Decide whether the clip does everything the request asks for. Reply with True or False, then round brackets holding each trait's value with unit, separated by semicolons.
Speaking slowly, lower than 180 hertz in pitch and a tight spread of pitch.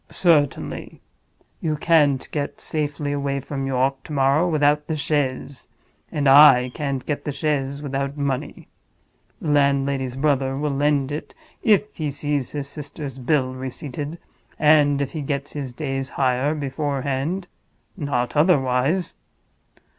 True (130 wpm; 140 Hz; 1.8 semitones)